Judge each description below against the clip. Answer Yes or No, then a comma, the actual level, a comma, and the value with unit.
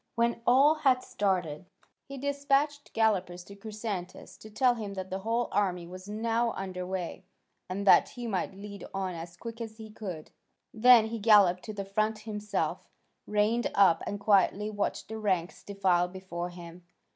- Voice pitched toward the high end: Yes, high, 205 Hz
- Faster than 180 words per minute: No, average, 170 wpm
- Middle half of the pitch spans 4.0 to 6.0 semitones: No, average, 3.5 semitones